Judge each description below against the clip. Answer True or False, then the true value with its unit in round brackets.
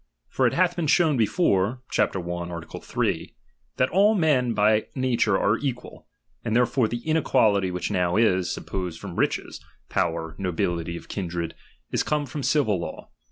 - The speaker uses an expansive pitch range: True (7.1 semitones)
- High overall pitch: False (110 Hz)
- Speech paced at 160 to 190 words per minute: True (165 wpm)